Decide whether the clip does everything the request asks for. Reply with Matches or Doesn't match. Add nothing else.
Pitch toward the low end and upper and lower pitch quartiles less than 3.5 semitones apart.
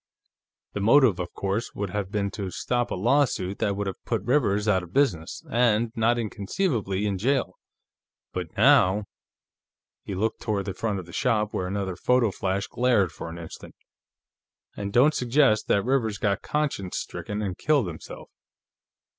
Doesn't match